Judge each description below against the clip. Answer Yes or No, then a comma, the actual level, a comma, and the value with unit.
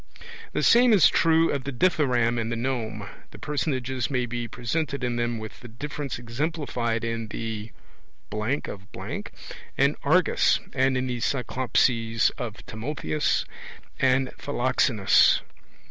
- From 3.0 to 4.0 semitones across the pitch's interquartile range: Yes, average, 3.3 semitones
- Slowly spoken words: Yes, slow, 130 wpm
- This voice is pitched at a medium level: No, low, 125 Hz